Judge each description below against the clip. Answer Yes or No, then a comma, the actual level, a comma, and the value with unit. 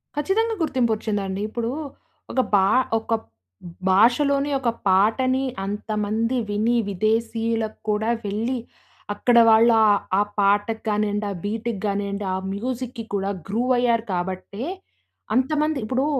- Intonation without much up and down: No, average, 3.4 semitones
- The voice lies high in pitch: Yes, high, 225 Hz